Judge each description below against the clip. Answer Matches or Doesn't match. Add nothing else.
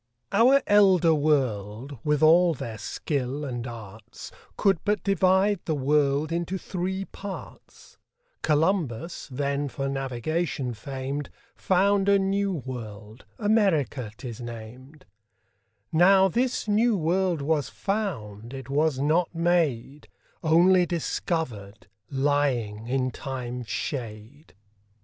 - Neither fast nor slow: Doesn't match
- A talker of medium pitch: Matches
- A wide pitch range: Matches